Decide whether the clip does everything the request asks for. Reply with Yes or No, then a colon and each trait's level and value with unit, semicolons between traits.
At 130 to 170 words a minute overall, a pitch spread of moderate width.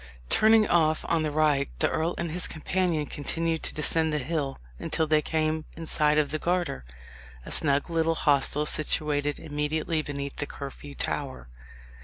No: average, 165 wpm; narrow, 1.9 semitones